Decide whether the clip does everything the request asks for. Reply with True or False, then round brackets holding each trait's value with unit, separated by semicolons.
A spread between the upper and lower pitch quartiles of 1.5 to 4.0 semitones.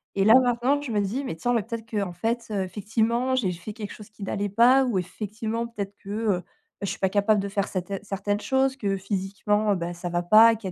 True (2.9 semitones)